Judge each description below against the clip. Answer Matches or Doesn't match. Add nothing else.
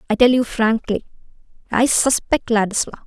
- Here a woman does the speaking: Matches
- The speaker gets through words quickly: Doesn't match